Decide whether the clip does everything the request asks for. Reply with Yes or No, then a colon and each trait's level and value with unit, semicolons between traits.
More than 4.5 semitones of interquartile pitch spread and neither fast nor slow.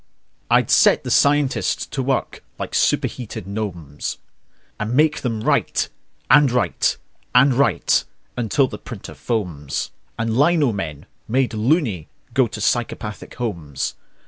No: average, 4.9 semitones; slow, 125 wpm